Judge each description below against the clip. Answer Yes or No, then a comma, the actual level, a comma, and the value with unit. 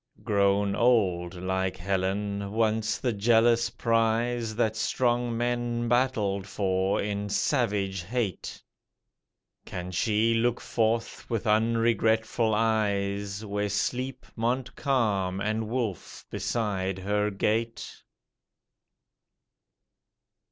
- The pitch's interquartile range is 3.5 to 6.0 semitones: No, average, 2.9 semitones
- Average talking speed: No, slow, 90 wpm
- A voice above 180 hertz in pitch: No, low, 110 Hz